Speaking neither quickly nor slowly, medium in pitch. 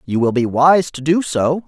No: fast, 250 wpm; medium, 145 Hz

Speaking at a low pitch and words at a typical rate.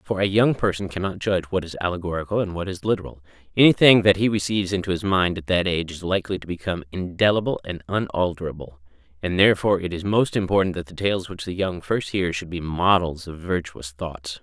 No: very low, 90 Hz; fast, 210 wpm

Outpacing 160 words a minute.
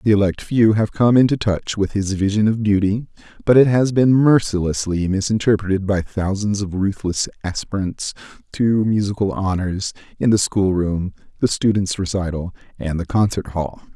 No: average, 155 wpm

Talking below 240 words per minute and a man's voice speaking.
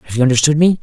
No: fast, 290 wpm; male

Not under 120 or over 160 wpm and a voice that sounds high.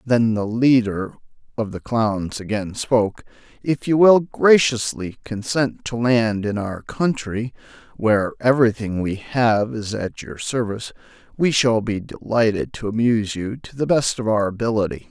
No: average, 155 wpm; low, 115 Hz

